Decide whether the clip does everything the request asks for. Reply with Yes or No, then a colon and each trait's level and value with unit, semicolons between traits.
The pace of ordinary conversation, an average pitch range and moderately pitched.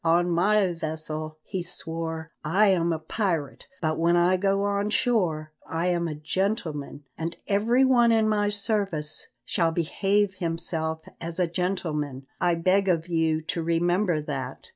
Yes: average, 155 wpm; average, 3.6 semitones; medium, 170 Hz